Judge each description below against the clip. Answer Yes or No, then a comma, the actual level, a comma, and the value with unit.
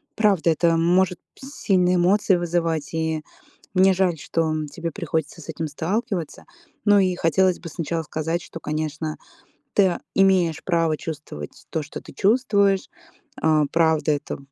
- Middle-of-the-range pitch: Yes, medium, 170 Hz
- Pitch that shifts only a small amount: No, average, 3.0 semitones